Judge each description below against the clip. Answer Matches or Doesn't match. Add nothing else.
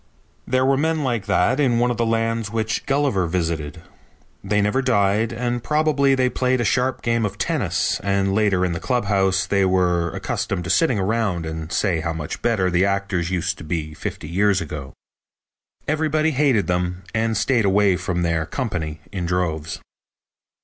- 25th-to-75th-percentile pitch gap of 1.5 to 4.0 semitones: Doesn't match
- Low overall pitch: Matches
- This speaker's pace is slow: Doesn't match